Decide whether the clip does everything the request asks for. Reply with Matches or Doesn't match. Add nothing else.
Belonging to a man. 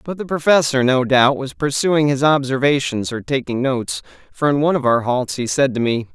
Matches